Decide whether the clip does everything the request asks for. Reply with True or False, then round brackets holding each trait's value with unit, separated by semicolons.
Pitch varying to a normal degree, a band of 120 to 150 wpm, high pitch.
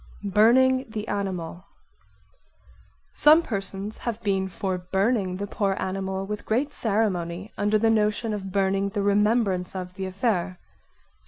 False (2.3 semitones; 135 wpm; 200 Hz)